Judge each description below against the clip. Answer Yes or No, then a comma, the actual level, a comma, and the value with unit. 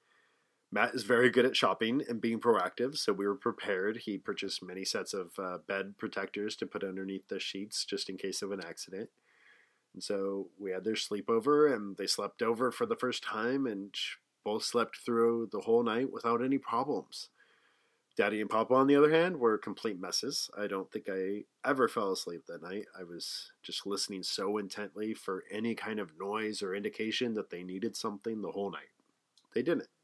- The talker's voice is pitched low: Yes, low, 105 Hz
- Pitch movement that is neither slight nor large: Yes, average, 3.0 semitones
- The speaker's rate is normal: Yes, average, 195 wpm